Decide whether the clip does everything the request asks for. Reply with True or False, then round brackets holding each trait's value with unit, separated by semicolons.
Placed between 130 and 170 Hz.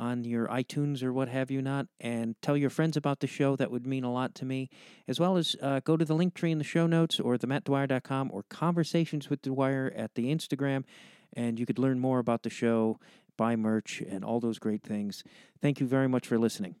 True (135 Hz)